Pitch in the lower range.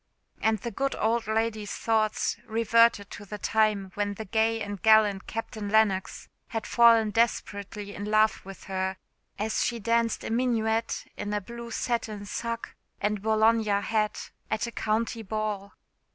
No: high, 220 Hz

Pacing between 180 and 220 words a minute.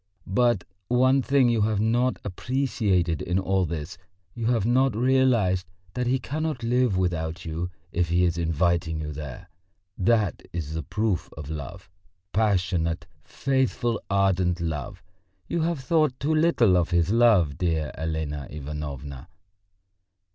No: average, 140 wpm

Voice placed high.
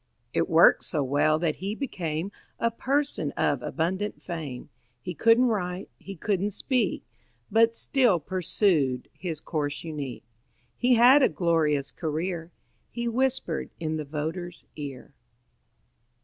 No: medium, 175 Hz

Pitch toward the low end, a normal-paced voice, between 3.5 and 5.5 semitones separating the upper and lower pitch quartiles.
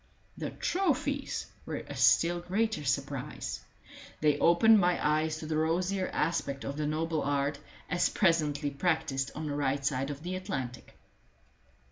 No: medium, 155 Hz; average, 145 wpm; average, 3.8 semitones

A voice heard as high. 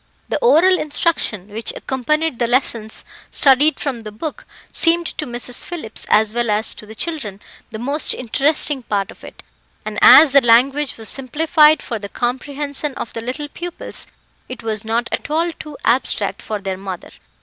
Yes: very high, 255 Hz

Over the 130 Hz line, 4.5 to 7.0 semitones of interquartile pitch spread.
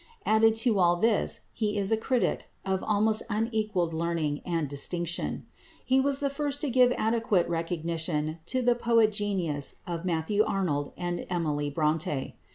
Yes: high, 190 Hz; average, 5.2 semitones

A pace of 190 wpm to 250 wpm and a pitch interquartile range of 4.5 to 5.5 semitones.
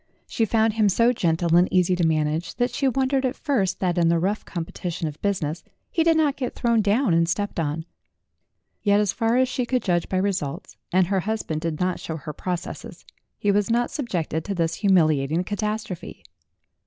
Yes: average, 195 wpm; average, 5.2 semitones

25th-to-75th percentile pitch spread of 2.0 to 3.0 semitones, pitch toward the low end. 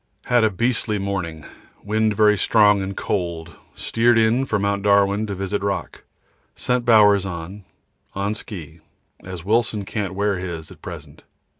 Yes: narrow, 2.4 semitones; low, 100 Hz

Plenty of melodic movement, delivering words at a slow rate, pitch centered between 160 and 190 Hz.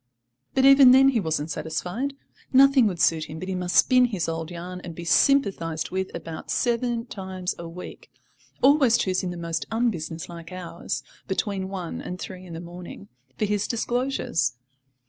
No: wide, 5.9 semitones; average, 165 wpm; medium, 185 Hz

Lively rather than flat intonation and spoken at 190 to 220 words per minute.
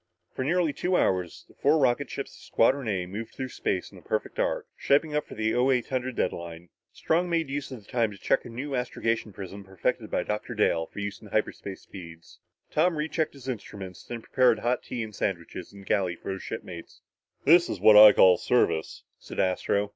Yes: wide, 5.8 semitones; fast, 205 wpm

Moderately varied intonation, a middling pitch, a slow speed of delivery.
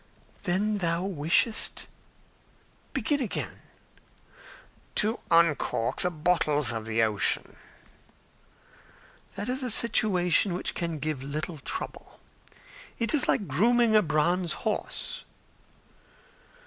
No: wide, 6.0 semitones; medium, 175 Hz; slow, 100 wpm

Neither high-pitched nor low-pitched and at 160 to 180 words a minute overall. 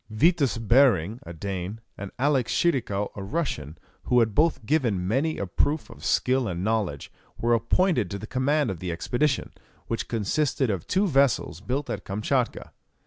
No: low, 115 Hz; average, 165 wpm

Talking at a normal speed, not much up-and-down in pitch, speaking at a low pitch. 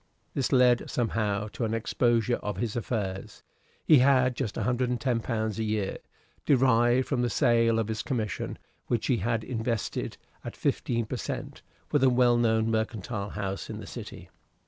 Yes: average, 160 wpm; narrow, 2.2 semitones; low, 115 Hz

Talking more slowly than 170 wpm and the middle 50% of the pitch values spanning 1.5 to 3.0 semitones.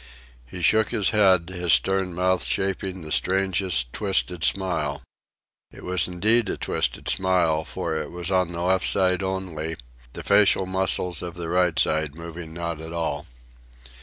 Yes: average, 160 wpm; narrow, 2.4 semitones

